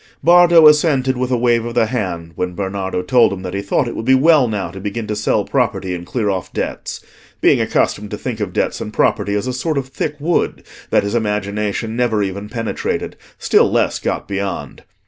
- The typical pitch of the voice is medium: No, low, 110 Hz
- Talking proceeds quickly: Yes, fast, 210 wpm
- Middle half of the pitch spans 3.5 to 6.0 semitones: Yes, average, 4.4 semitones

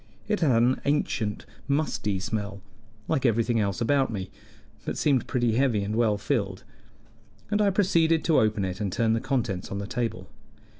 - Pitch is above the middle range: No, low, 115 Hz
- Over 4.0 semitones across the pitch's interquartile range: Yes, average, 5.3 semitones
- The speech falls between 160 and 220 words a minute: Yes, average, 170 wpm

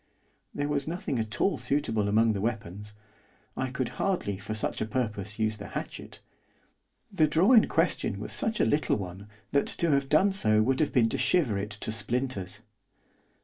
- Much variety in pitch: Yes, wide, 5.8 semitones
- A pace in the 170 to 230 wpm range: Yes, average, 185 wpm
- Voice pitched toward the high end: No, low, 115 Hz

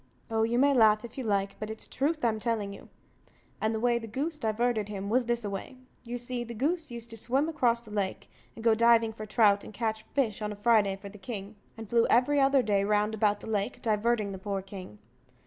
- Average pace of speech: No, fast, 235 wpm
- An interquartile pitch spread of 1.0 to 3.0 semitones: Yes, narrow, 2.4 semitones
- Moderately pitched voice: No, high, 220 Hz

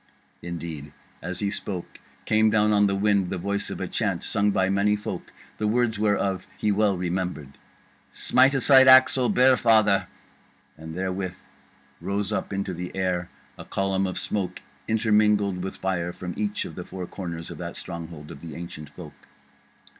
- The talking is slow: No, average, 170 wpm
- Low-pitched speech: Yes, very low, 95 Hz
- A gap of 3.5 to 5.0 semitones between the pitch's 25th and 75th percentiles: No, average, 3.0 semitones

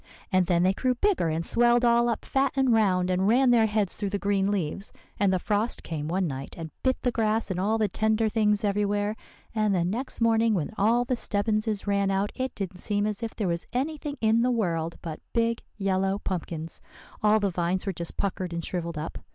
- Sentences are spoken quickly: Yes, fast, 215 wpm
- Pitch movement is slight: No, average, 3.7 semitones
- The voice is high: Yes, high, 205 Hz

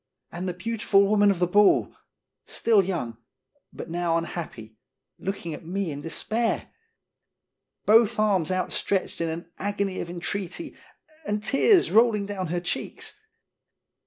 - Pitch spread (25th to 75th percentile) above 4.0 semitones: No, average, 3.3 semitones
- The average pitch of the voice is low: No, high, 190 Hz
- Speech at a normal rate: No, slow, 130 wpm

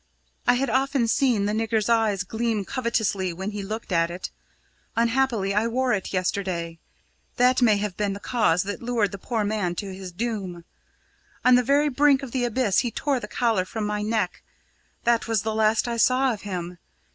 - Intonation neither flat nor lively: Yes, average, 3.6 semitones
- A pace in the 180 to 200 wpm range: Yes, average, 195 wpm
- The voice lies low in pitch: No, high, 220 Hz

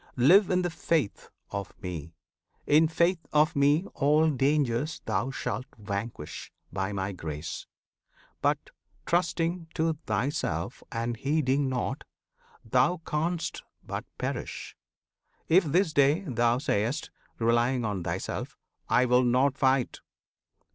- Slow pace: Yes, slow, 120 wpm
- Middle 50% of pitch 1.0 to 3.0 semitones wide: No, wide, 5.5 semitones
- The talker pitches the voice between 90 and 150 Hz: Yes, low, 135 Hz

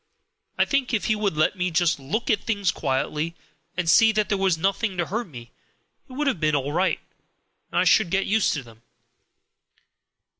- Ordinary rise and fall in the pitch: No, wide, 5.7 semitones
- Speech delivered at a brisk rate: Yes, fast, 210 wpm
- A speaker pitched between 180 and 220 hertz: Yes, medium, 185 Hz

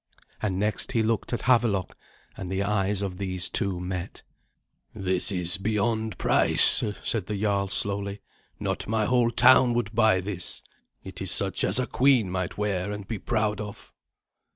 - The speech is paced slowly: No, average, 165 wpm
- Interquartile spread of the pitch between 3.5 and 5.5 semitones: No, average, 2.7 semitones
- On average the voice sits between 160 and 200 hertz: No, low, 100 Hz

